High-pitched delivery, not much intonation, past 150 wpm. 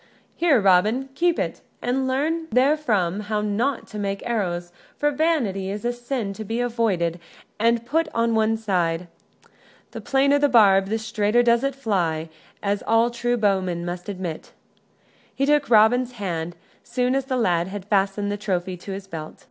No: high, 220 Hz; average, 4.4 semitones; average, 170 wpm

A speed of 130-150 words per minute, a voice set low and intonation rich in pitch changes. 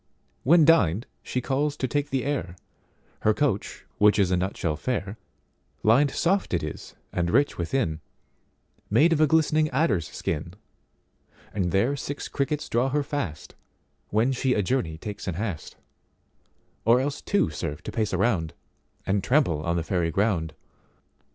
Yes: average, 140 wpm; low, 110 Hz; wide, 8.1 semitones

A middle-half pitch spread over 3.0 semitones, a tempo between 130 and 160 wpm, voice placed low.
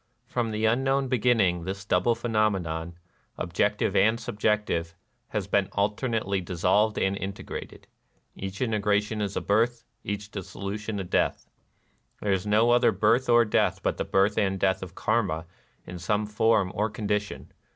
No: narrow, 2.6 semitones; average, 150 wpm; low, 105 Hz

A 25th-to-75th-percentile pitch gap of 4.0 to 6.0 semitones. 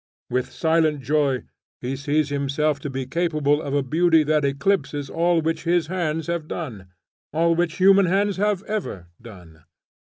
No: average, 3.6 semitones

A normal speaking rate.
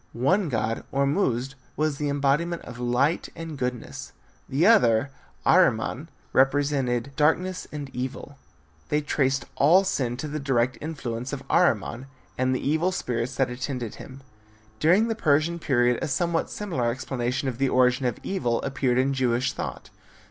Yes: average, 150 wpm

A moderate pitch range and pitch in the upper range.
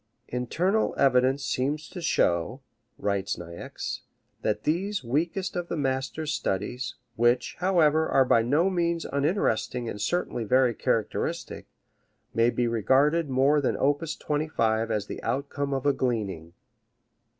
No: average, 5.0 semitones; low, 135 Hz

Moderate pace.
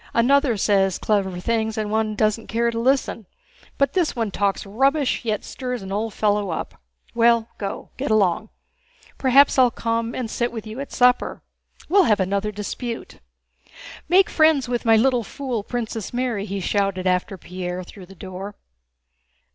Yes: average, 165 wpm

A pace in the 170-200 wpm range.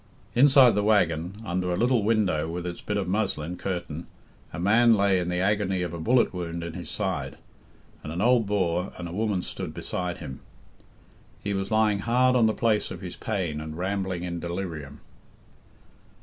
Yes: average, 185 wpm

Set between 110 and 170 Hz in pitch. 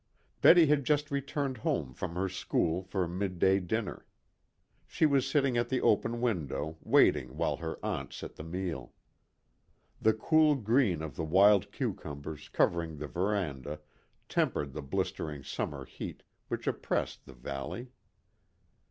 No: very low, 95 Hz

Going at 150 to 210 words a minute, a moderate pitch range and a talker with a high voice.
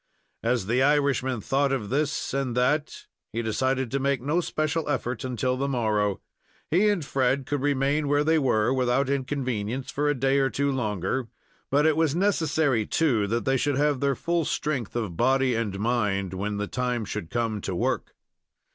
No: average, 180 wpm; average, 3.7 semitones; low, 130 Hz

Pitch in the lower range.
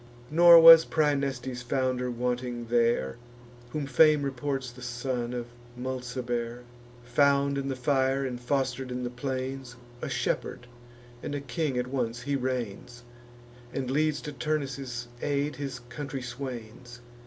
Yes: low, 130 Hz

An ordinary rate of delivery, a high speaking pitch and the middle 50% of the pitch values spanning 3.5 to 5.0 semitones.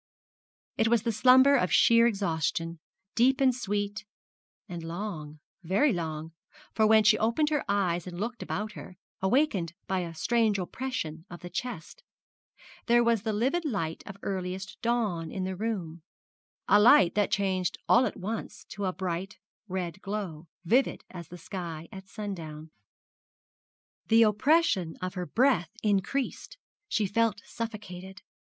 Yes: average, 145 wpm; high, 200 Hz; average, 4.5 semitones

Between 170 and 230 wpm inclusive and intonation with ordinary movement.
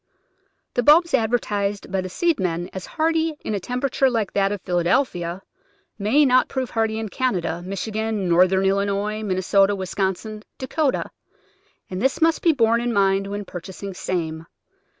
No: average, 150 wpm; average, 4.6 semitones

